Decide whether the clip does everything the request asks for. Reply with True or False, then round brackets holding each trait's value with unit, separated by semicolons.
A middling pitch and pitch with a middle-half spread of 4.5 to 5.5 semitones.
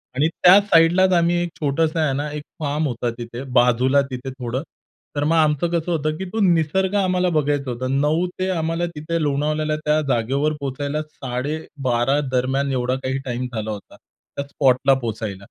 False (145 Hz; 3.9 semitones)